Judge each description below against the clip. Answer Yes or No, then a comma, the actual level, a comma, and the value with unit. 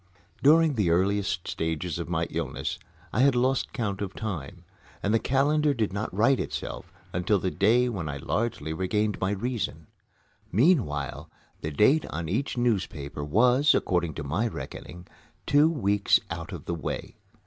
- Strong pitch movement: Yes, wide, 6.5 semitones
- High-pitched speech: No, low, 100 Hz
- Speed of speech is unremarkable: Yes, average, 160 wpm